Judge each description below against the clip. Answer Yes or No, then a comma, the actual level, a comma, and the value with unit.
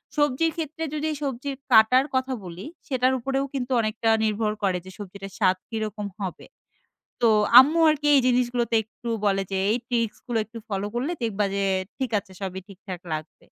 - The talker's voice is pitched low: No, high, 230 Hz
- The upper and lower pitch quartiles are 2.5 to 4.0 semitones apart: No, average, 4.7 semitones